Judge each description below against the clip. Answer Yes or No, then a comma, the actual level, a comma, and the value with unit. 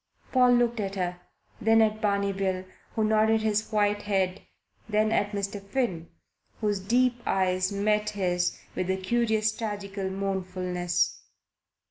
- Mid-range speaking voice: No, high, 205 Hz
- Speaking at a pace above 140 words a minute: No, slow, 135 wpm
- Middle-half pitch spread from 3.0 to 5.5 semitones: No, narrow, 2.4 semitones